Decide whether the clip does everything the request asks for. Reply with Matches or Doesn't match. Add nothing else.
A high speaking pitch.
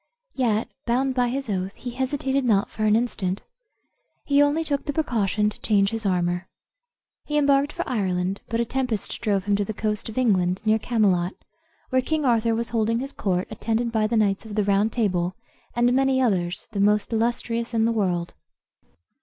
Matches